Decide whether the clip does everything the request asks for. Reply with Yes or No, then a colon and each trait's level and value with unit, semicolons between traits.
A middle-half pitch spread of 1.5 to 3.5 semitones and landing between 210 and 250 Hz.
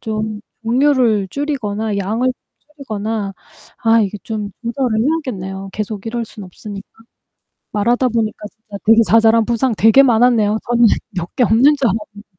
Yes: average, 2.7 semitones; high, 220 Hz